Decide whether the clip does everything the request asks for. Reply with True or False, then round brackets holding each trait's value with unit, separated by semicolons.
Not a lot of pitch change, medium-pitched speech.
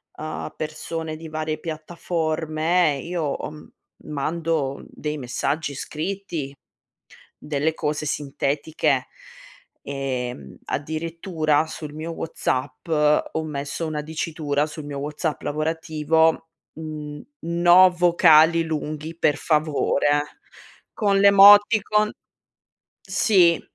True (2.0 semitones; 155 Hz)